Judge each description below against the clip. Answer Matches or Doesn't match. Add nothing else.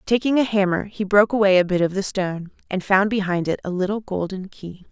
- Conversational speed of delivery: Doesn't match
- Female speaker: Matches